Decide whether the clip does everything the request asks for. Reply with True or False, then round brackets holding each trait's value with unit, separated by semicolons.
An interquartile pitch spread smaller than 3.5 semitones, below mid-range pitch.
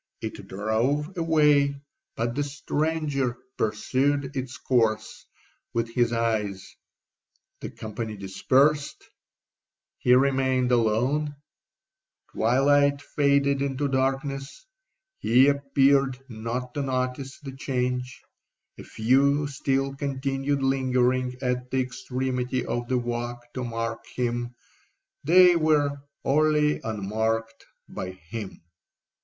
True (2.8 semitones; 130 Hz)